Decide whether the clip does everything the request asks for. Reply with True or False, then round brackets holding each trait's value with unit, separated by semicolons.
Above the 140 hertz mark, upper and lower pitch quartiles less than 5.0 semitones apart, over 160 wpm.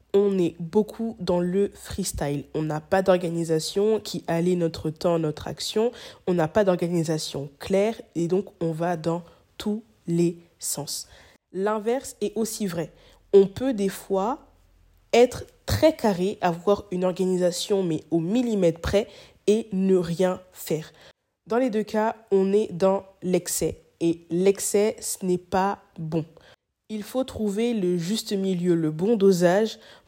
False (185 Hz; 3.7 semitones; 150 wpm)